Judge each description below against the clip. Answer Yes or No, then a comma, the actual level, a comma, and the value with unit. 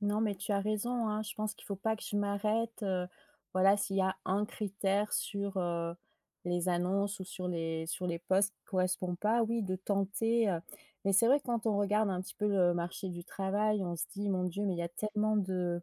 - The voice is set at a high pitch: Yes, high, 200 Hz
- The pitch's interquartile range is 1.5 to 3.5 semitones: Yes, narrow, 2.6 semitones